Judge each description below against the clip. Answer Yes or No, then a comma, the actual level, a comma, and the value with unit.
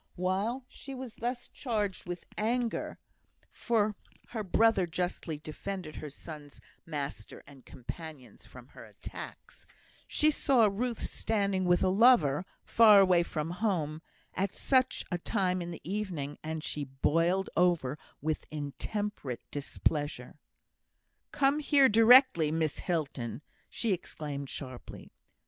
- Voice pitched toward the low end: No, medium, 180 Hz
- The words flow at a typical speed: No, slow, 125 wpm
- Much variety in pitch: Yes, wide, 6.3 semitones